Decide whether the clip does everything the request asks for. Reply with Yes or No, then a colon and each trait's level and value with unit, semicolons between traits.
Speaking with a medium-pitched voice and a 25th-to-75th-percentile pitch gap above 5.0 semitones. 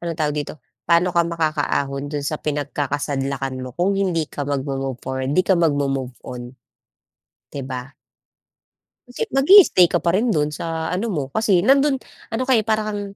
Yes: medium, 155 Hz; wide, 5.6 semitones